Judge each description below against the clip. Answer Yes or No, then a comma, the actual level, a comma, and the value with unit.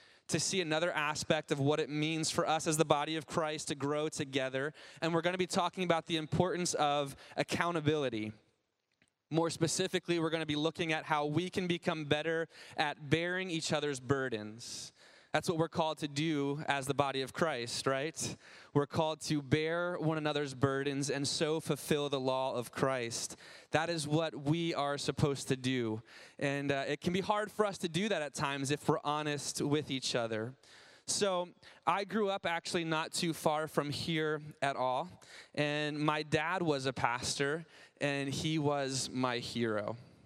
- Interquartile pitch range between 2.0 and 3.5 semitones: Yes, average, 2.8 semitones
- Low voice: No, medium, 150 Hz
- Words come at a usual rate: Yes, average, 180 wpm